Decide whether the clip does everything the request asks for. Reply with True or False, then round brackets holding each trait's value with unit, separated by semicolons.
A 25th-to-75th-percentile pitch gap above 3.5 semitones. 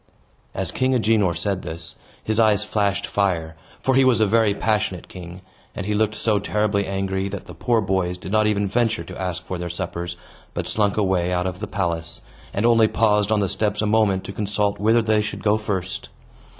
False (2.7 semitones)